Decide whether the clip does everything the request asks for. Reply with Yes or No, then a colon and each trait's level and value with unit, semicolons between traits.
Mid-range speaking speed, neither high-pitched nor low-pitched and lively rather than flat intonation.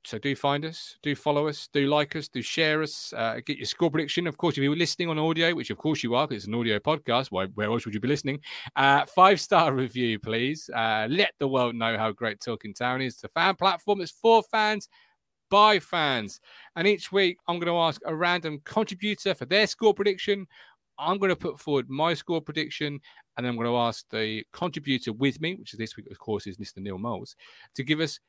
No: fast, 235 wpm; medium, 150 Hz; wide, 6.3 semitones